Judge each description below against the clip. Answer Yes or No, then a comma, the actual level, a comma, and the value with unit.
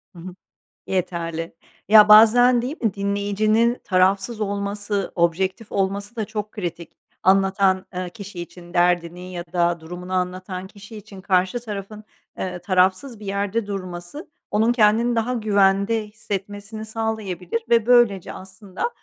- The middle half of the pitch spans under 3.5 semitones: Yes, average, 2.8 semitones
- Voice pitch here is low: No, high, 200 Hz